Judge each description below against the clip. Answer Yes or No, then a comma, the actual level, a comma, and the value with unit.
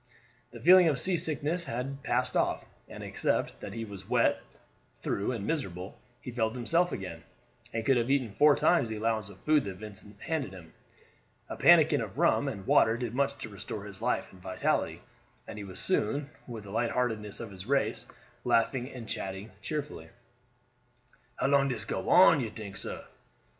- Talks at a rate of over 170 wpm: Yes, average, 180 wpm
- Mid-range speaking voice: No, low, 115 Hz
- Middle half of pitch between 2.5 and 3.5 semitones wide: No, wide, 5.5 semitones